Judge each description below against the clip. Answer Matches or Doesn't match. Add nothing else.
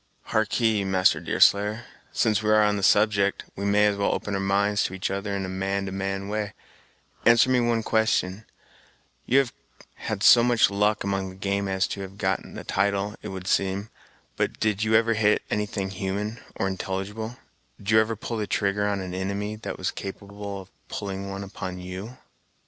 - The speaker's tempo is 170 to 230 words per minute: Matches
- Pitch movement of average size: Doesn't match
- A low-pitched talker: Matches